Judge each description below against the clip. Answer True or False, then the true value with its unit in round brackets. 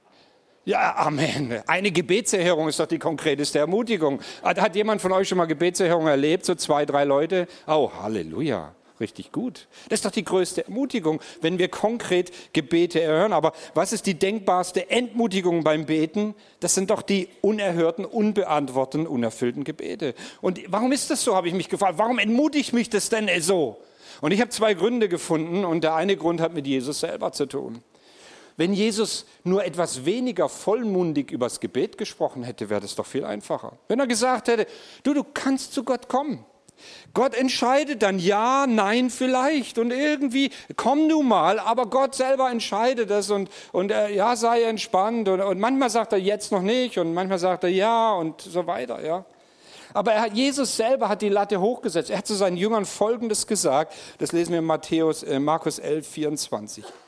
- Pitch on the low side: False (195 Hz)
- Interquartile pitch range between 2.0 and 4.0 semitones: False (5.6 semitones)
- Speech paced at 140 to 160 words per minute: False (185 wpm)